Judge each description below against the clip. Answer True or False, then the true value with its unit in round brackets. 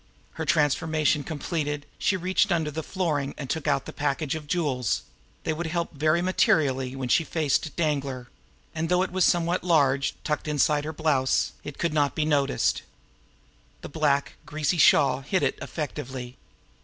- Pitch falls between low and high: True (150 Hz)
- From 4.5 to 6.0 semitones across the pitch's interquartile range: False (2.8 semitones)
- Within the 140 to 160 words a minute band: False (170 wpm)